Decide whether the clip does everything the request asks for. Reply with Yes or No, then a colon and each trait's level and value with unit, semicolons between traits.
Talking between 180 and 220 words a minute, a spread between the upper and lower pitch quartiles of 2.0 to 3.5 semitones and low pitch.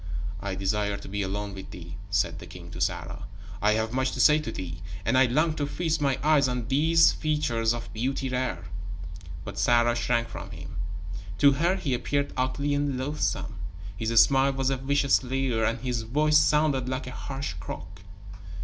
No: average, 185 wpm; average, 4.3 semitones; low, 130 Hz